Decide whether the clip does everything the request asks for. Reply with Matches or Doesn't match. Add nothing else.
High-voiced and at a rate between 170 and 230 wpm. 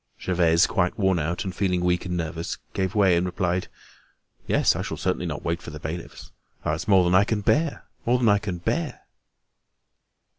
Doesn't match